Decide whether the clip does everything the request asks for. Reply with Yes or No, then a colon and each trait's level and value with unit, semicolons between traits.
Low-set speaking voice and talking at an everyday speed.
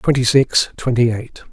Yes: low, 125 Hz; average, 160 wpm